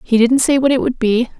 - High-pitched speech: Yes, very high, 250 Hz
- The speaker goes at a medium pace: No, fast, 300 wpm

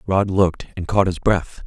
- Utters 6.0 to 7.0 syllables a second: No, 4.9 syllables/s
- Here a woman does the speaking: No, male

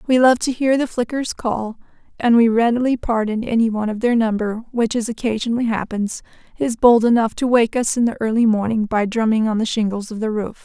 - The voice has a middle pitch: No, high, 230 Hz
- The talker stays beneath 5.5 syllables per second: No, 5.8 syllables/s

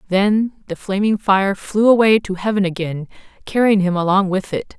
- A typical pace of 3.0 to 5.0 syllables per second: Yes, 4.8 syllables/s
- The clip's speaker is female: Yes, female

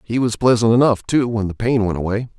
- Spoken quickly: Yes, fast, 250 wpm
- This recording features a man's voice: Yes, male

